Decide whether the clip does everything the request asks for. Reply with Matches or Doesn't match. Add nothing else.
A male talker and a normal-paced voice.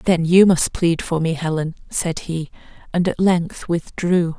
Doesn't match